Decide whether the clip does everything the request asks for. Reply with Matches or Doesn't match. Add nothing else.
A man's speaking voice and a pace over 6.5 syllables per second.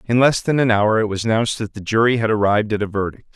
Matches